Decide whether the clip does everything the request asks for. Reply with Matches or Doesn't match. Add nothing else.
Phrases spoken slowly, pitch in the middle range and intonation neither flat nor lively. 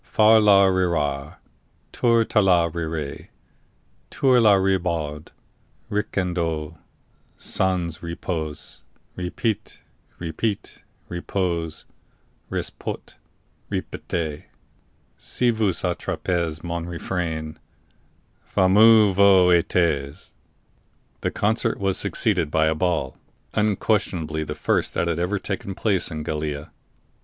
Doesn't match